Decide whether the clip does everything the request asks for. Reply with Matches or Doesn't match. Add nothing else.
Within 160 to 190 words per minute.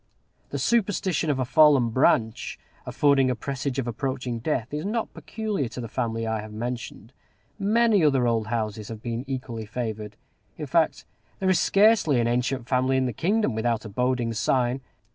Matches